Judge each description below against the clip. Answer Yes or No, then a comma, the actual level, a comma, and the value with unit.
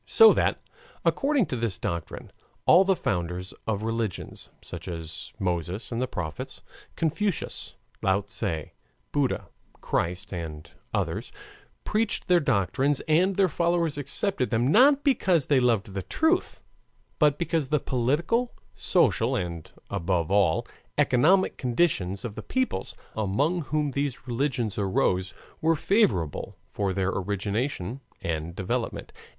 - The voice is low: Yes, low, 120 Hz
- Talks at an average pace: No, slow, 130 wpm